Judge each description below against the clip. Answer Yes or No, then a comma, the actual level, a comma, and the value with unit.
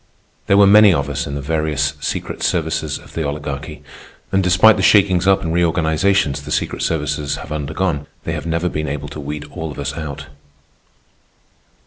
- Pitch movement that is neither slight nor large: Yes, average, 3.4 semitones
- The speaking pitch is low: Yes, very low, 80 Hz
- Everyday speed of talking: Yes, average, 180 wpm